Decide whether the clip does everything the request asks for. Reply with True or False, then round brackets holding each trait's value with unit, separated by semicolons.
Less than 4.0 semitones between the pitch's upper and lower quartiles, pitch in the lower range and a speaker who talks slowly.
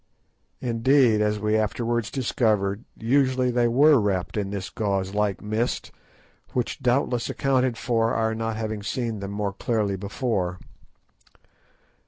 True (3.1 semitones; 110 Hz; 130 wpm)